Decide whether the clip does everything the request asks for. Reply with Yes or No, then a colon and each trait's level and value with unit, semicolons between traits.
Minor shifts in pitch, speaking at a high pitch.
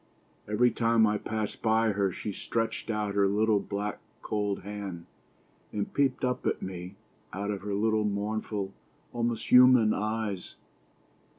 No: narrow, 1.8 semitones; low, 105 Hz